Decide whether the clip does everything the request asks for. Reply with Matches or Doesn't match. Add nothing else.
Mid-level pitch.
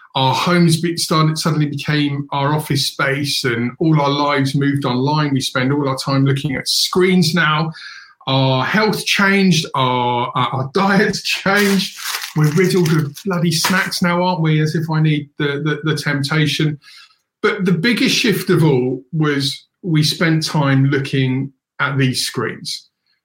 Matches